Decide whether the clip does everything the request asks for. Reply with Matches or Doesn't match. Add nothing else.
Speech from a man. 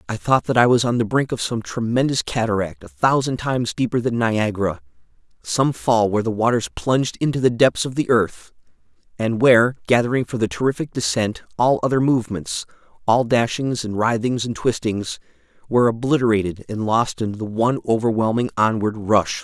Matches